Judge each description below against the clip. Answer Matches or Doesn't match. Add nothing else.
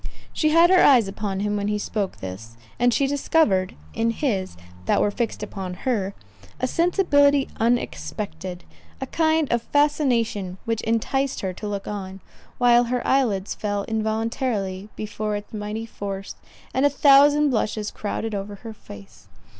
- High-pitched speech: Matches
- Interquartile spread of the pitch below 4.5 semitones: Doesn't match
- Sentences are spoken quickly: Doesn't match